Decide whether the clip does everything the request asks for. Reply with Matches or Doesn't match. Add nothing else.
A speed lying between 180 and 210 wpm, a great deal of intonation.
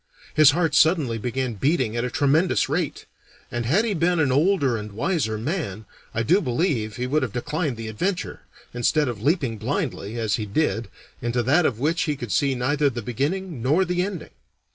Matches